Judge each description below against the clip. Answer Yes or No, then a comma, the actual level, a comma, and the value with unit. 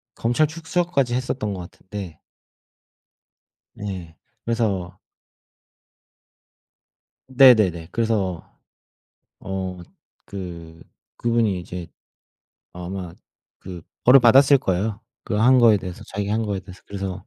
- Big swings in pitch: No, average, 4.5 semitones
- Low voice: Yes, low, 100 Hz